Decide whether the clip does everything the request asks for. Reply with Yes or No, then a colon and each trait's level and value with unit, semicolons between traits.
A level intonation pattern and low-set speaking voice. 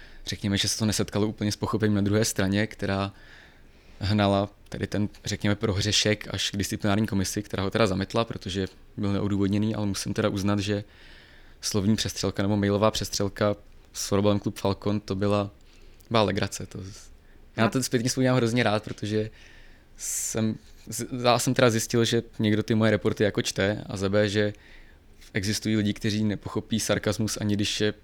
Yes: narrow, 1.7 semitones; low, 105 Hz